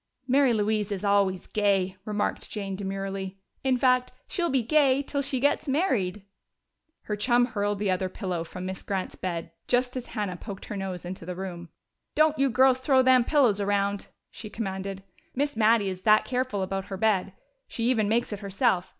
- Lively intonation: No, average, 4.8 semitones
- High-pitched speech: Yes, high, 205 Hz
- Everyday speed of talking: Yes, average, 185 wpm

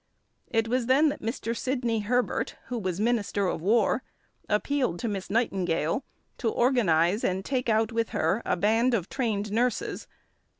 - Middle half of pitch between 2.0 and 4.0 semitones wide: Yes, average, 3.6 semitones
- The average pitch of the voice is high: Yes, high, 225 Hz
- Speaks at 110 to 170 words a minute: Yes, average, 160 wpm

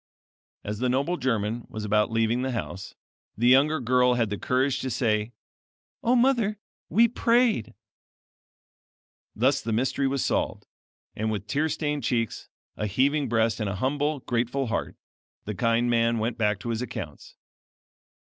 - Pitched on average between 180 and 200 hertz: No, low, 120 Hz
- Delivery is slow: No, average, 155 wpm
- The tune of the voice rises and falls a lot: No, average, 3.9 semitones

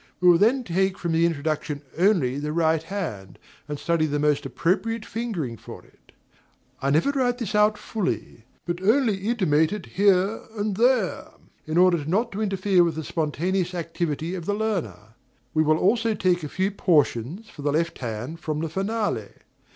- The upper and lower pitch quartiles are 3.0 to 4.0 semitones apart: No, average, 5.1 semitones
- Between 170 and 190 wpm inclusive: Yes, average, 175 wpm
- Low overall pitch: No, medium, 175 Hz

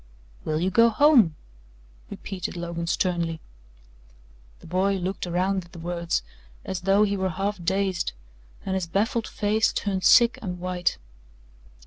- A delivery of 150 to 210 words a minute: No, average, 140 wpm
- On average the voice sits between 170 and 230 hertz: Yes, medium, 185 Hz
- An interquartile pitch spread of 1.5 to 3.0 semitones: Yes, narrow, 2.5 semitones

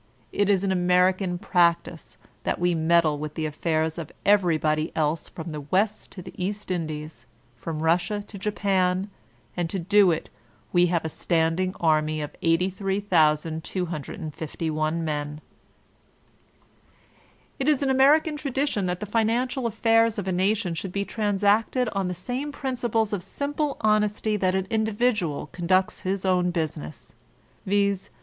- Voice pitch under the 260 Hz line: Yes, medium, 185 Hz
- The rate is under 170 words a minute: Yes, average, 140 wpm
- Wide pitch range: No, average, 4.3 semitones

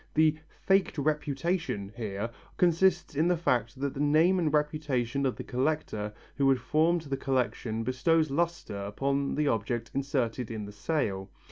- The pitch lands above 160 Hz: No, medium, 140 Hz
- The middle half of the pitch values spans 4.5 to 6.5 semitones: Yes, average, 5.0 semitones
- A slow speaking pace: No, average, 155 wpm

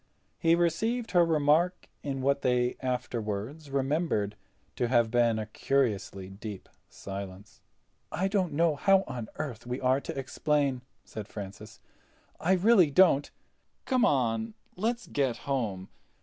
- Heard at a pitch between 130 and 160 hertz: Yes, low, 135 Hz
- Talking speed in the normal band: No, slow, 130 wpm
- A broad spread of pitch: Yes, wide, 6.8 semitones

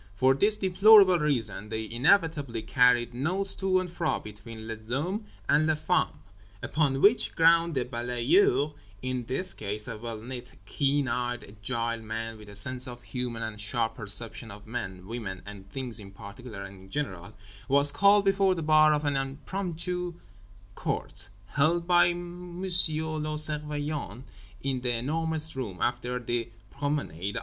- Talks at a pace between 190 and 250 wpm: No, average, 150 wpm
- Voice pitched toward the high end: No, low, 130 Hz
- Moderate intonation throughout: No, wide, 5.9 semitones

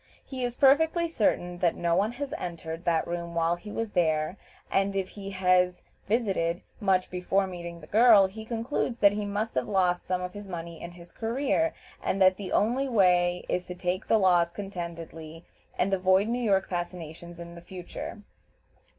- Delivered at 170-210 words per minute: Yes, average, 180 wpm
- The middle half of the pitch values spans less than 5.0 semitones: Yes, average, 3.3 semitones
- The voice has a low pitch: No, medium, 185 Hz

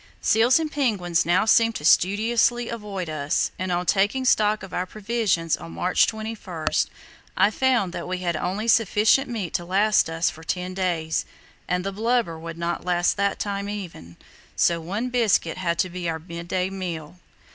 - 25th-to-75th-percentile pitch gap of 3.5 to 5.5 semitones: Yes, average, 4.2 semitones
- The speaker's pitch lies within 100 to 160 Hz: No, medium, 185 Hz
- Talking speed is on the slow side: No, average, 175 wpm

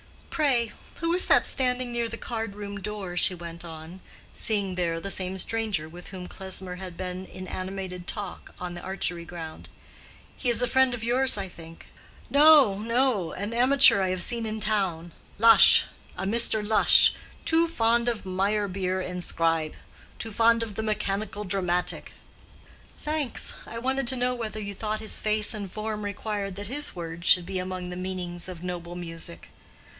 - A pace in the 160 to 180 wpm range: Yes, average, 170 wpm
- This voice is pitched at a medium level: No, high, 200 Hz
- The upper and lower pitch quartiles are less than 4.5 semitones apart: Yes, average, 4.1 semitones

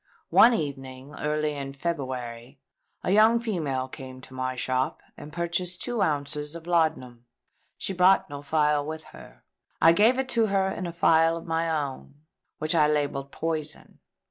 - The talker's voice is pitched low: No, medium, 155 Hz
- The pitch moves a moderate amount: Yes, average, 3.8 semitones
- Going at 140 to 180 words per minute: Yes, average, 165 wpm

